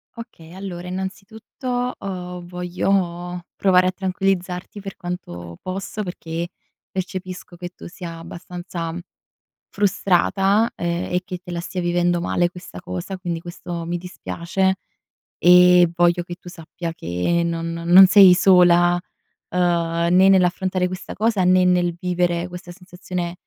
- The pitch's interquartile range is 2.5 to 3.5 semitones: No, narrow, 1.3 semitones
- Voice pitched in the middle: Yes, medium, 180 Hz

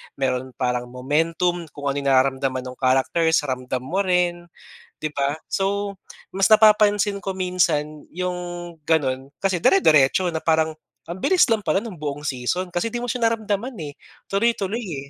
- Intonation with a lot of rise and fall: Yes, wide, 6.3 semitones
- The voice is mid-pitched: Yes, medium, 165 Hz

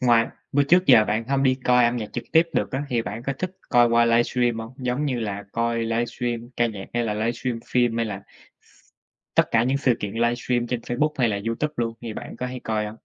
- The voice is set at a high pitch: No, low, 120 Hz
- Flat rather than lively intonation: Yes, narrow, 1.8 semitones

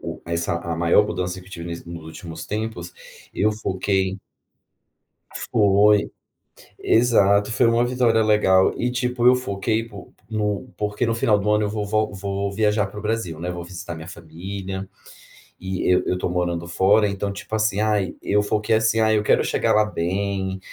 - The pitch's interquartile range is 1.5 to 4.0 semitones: Yes, average, 2.8 semitones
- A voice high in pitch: No, low, 100 Hz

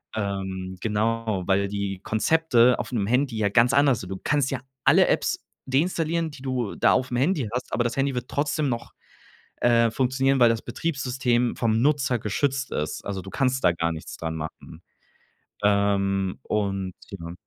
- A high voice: No, low, 115 Hz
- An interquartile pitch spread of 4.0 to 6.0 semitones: Yes, average, 5.1 semitones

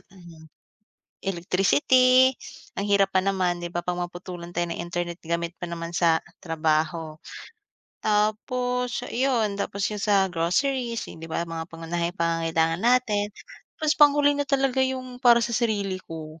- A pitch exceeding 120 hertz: Yes, medium, 185 Hz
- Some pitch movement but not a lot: No, wide, 6.2 semitones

